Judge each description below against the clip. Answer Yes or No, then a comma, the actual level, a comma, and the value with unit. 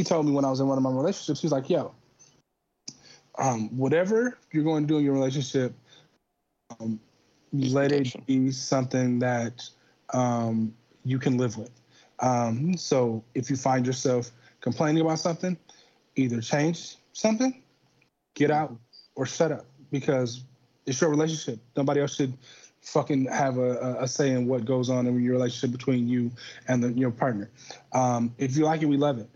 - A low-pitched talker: Yes, low, 130 Hz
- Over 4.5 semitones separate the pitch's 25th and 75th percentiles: No, average, 3.0 semitones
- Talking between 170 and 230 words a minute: Yes, average, 175 wpm